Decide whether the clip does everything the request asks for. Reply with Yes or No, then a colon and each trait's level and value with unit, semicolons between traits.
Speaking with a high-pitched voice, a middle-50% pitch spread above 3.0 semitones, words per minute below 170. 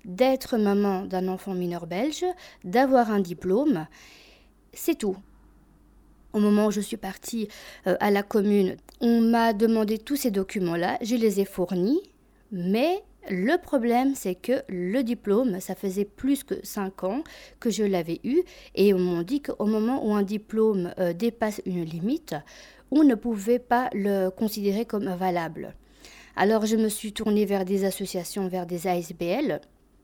Yes: high, 210 Hz; average, 4.2 semitones; average, 155 wpm